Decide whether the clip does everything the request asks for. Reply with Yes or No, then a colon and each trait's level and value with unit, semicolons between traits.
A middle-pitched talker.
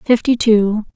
No: high, 220 Hz